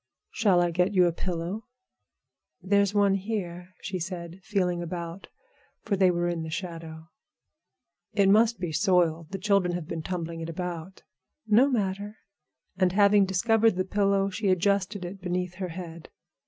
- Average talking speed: Yes, average, 155 wpm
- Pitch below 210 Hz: Yes, medium, 185 Hz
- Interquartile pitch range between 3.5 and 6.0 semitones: No, narrow, 2.6 semitones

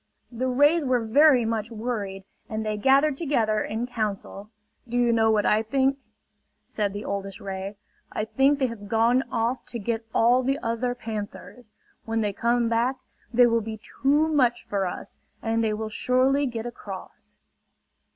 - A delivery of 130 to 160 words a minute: No, average, 170 wpm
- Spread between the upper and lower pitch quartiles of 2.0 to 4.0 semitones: Yes, average, 2.9 semitones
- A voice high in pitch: Yes, high, 230 Hz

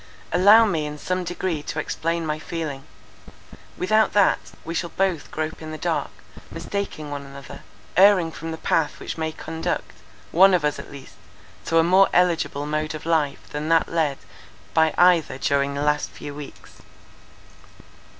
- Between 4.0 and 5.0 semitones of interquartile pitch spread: No, average, 3.0 semitones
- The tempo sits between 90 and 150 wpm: No, average, 165 wpm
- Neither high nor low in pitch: Yes, medium, 160 Hz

